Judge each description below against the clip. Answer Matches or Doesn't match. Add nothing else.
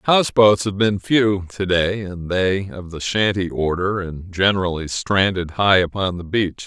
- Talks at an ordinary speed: Matches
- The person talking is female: Doesn't match